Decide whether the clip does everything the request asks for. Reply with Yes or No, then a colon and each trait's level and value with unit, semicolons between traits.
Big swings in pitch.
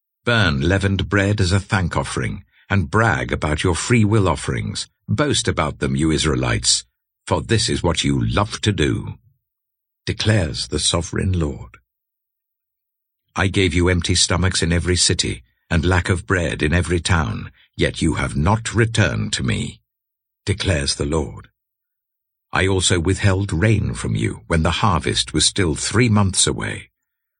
No: average, 4.1 semitones